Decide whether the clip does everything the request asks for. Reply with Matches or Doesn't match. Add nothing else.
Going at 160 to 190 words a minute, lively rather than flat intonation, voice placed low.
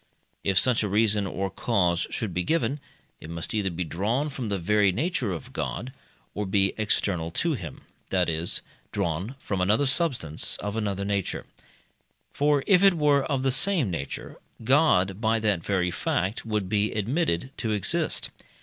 Matches